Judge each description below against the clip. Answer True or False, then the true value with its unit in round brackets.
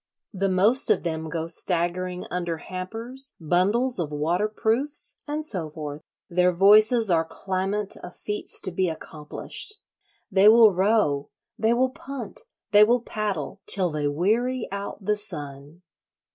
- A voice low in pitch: False (190 Hz)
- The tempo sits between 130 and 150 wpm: True (140 wpm)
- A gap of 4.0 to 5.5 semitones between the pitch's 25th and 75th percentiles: True (4.7 semitones)